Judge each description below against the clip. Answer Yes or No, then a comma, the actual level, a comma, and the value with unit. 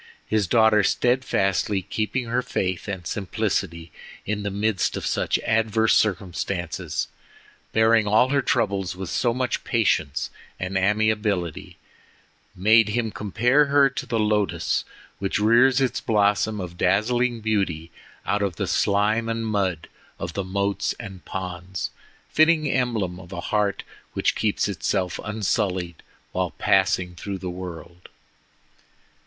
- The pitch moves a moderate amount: Yes, average, 3.2 semitones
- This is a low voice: Yes, low, 105 Hz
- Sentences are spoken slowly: Yes, slow, 125 wpm